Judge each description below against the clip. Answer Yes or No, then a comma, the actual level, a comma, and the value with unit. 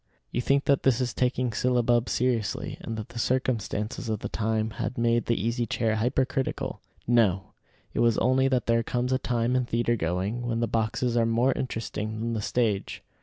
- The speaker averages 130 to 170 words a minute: No, average, 190 wpm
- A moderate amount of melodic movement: No, narrow, 2.0 semitones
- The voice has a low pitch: Yes, low, 115 Hz